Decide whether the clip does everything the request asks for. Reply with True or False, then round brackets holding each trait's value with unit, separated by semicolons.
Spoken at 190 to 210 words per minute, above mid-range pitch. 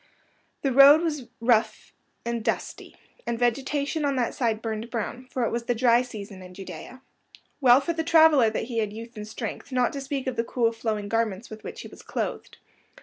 True (205 wpm; 240 Hz)